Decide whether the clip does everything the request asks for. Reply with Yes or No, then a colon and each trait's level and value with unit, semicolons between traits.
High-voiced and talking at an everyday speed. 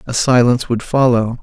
No: low, 120 Hz; average, 170 wpm